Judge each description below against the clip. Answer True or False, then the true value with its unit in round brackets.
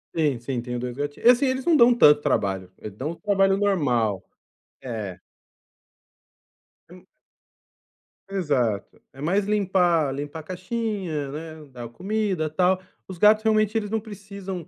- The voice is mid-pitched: True (170 Hz)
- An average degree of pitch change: False (7.1 semitones)